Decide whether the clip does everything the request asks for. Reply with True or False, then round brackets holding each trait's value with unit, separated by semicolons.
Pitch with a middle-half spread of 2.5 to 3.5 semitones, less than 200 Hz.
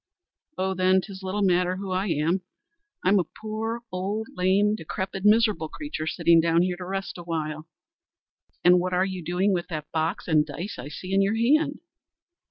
True (3.0 semitones; 185 Hz)